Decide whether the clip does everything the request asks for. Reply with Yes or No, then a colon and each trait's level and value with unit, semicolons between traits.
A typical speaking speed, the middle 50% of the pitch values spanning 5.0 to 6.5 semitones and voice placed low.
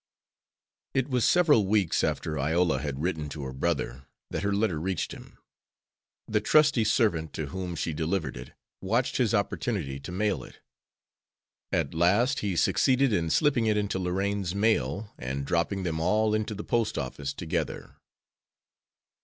Yes: average, 155 wpm; average, 5.3 semitones; very low, 95 Hz